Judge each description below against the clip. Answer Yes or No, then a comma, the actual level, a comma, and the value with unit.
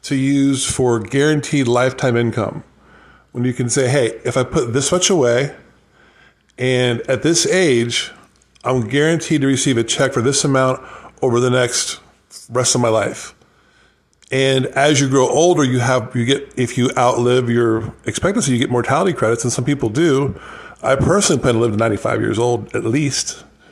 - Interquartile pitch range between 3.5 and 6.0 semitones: No, narrow, 2.4 semitones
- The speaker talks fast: No, average, 175 wpm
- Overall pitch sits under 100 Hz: No, low, 130 Hz